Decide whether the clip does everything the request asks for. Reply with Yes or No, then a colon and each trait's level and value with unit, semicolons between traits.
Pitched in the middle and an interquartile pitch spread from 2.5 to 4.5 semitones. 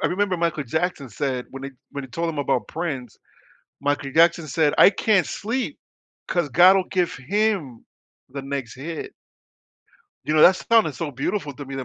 No: medium, 155 Hz; average, 4.9 semitones